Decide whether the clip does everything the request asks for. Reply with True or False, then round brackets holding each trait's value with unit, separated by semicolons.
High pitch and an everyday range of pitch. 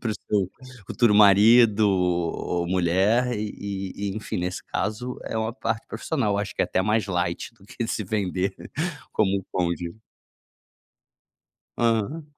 False (100 Hz; 3.1 semitones)